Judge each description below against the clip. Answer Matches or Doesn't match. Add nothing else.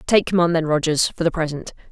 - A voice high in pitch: Doesn't match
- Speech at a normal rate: Doesn't match